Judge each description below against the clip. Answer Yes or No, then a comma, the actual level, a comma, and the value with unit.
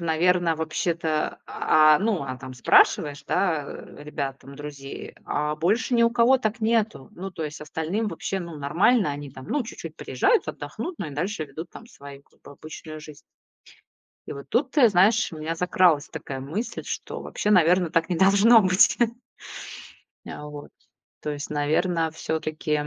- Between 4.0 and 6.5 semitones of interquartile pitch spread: Yes, average, 5.1 semitones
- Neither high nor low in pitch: Yes, medium, 160 Hz